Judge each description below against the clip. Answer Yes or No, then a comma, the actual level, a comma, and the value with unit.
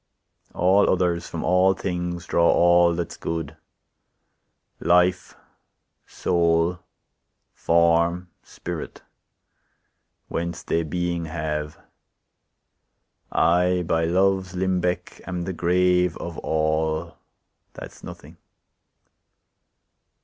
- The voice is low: Yes, very low, 85 Hz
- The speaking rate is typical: No, slow, 85 wpm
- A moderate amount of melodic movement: No, narrow, 1.4 semitones